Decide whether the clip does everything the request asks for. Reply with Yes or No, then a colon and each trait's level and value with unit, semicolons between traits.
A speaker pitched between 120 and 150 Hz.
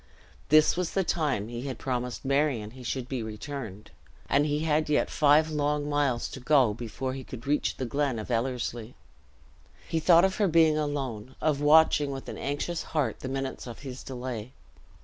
Yes: low, 135 Hz